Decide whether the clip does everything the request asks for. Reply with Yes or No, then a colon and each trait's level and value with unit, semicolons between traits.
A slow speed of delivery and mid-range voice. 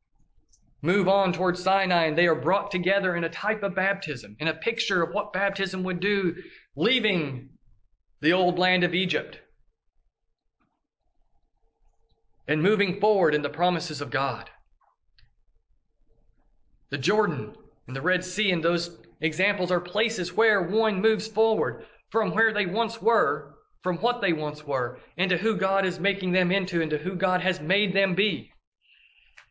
No: average, 150 wpm; medium, 180 Hz